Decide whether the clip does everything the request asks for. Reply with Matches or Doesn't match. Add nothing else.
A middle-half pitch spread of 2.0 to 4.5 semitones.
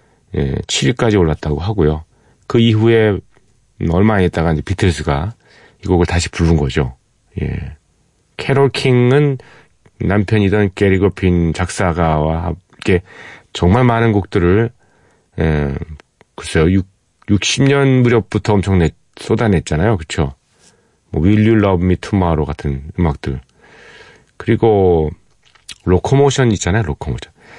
Doesn't match